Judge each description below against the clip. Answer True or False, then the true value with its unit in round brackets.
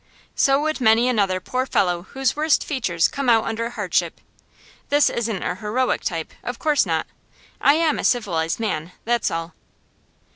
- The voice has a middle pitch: False (230 Hz)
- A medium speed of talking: True (160 wpm)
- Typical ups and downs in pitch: False (6.4 semitones)